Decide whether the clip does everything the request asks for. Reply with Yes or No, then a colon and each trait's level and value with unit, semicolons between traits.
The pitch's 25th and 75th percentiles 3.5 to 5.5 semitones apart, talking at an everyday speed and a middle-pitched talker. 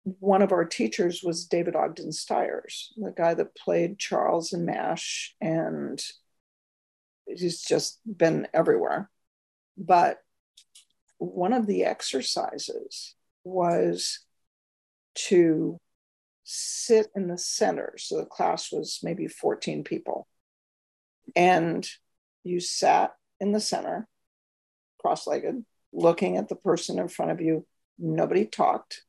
No: average, 4.5 semitones; slow, 115 wpm; medium, 180 Hz